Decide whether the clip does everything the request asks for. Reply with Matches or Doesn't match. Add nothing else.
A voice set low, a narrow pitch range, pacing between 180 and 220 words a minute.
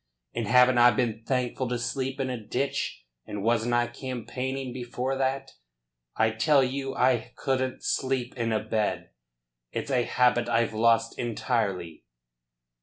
Doesn't match